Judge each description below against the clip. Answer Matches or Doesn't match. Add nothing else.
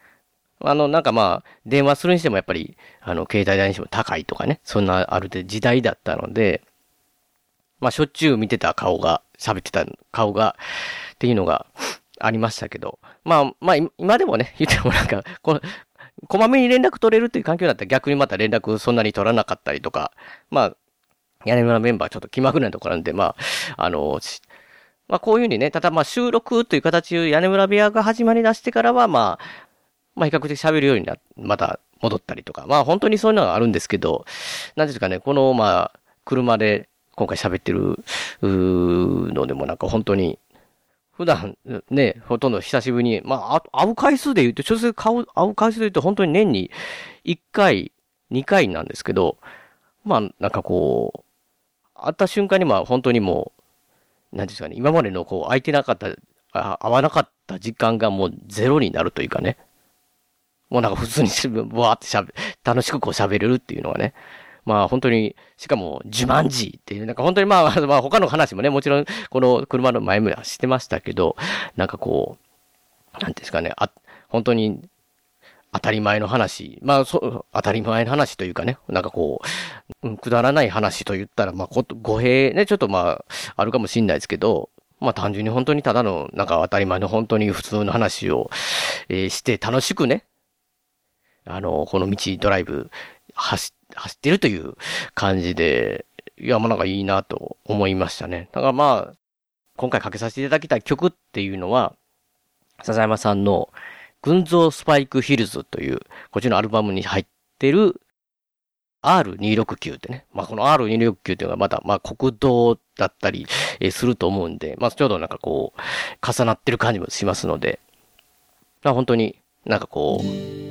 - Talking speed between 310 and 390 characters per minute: Matches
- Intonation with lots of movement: Matches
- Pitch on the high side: Doesn't match